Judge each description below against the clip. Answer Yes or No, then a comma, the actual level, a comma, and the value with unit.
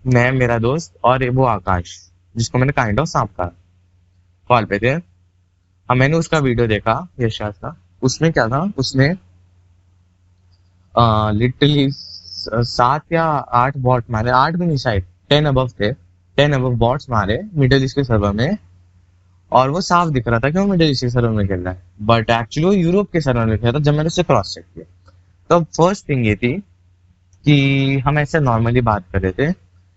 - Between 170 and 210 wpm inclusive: Yes, average, 175 wpm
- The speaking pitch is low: Yes, low, 120 Hz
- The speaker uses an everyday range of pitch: No, wide, 7.2 semitones